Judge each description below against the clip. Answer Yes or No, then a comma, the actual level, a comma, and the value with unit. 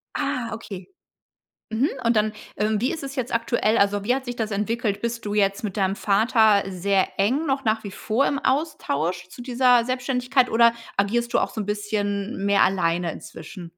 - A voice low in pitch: No, high, 220 Hz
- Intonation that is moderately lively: Yes, average, 3.5 semitones